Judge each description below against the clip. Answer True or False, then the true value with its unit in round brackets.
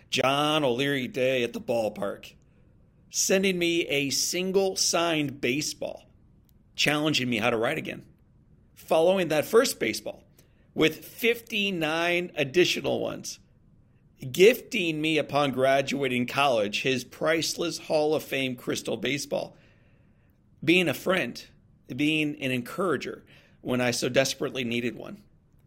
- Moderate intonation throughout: True (4.2 semitones)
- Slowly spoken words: True (115 wpm)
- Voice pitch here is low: False (150 Hz)